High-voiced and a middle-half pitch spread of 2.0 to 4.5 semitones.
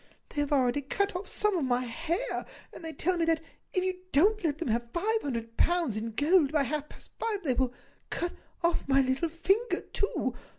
No: very high, 315 Hz; wide, 5.6 semitones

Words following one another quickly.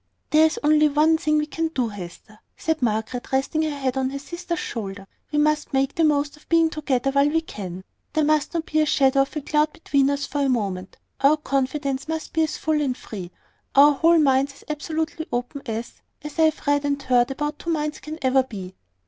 Yes: fast, 220 wpm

